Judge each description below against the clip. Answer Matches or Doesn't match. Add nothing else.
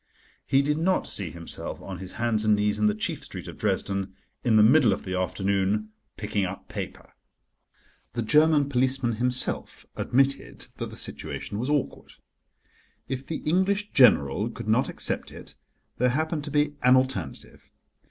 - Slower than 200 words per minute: Matches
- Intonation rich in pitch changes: Matches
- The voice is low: Matches